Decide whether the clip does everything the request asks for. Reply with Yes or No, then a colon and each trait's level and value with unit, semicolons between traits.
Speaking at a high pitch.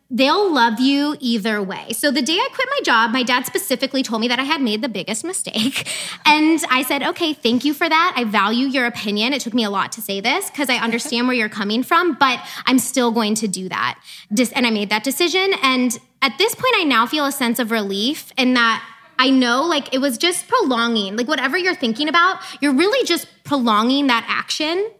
Yes: very high, 260 Hz